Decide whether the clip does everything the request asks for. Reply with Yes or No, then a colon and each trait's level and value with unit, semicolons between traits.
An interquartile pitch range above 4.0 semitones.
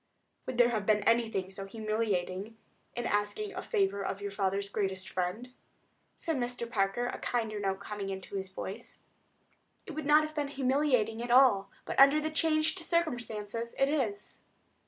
Yes: average, 5.3 semitones